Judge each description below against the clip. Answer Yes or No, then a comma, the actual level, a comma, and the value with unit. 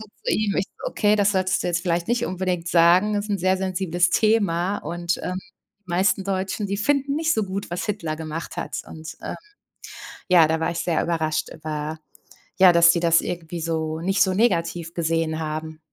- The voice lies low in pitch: No, medium, 175 Hz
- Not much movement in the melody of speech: No, average, 3.1 semitones